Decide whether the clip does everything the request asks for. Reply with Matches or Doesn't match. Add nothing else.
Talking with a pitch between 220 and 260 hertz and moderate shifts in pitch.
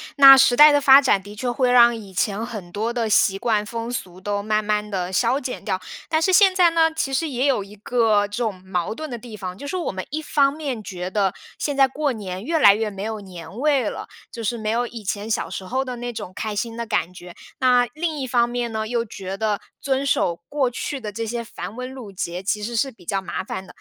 Matches